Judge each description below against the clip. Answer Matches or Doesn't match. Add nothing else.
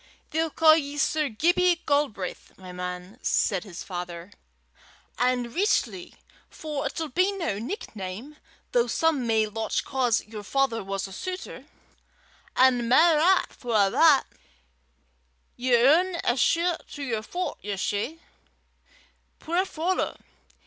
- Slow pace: Matches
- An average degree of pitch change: Doesn't match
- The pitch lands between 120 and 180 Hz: Doesn't match